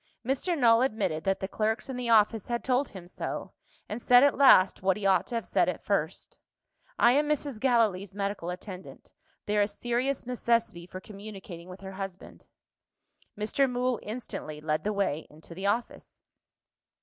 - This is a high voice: Yes, high, 210 Hz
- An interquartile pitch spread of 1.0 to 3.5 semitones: No, average, 4.4 semitones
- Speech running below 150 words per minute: No, average, 175 wpm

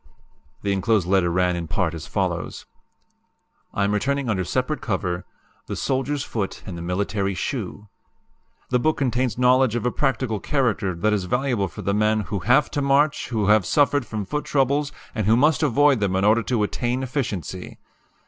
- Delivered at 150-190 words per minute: Yes, average, 180 wpm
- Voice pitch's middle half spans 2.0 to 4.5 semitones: No, average, 5.2 semitones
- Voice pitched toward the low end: Yes, low, 110 Hz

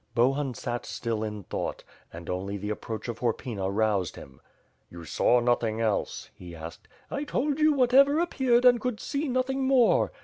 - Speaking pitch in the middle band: No, low, 120 Hz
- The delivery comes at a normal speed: Yes, average, 175 wpm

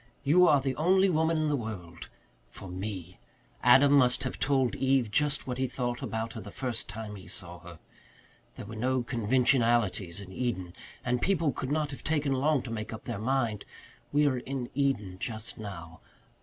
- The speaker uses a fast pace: No, average, 185 wpm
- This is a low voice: Yes, low, 125 Hz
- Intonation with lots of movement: No, average, 4.6 semitones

